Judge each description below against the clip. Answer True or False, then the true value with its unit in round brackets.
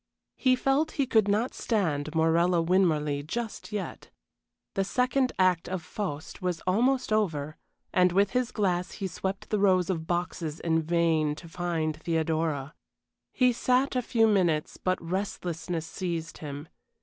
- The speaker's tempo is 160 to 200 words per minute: False (150 wpm)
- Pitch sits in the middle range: True (180 Hz)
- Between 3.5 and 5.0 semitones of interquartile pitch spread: True (4.5 semitones)